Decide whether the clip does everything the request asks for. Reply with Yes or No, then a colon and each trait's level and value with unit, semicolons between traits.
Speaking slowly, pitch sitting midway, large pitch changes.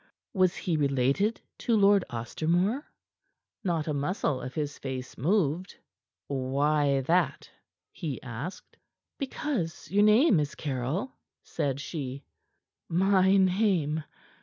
Yes: slow, 110 wpm; medium, 160 Hz; wide, 5.8 semitones